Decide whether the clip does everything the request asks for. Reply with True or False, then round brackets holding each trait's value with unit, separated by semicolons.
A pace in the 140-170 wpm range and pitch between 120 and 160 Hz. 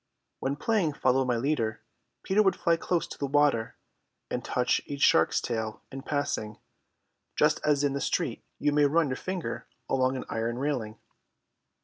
True (165 wpm; 140 Hz)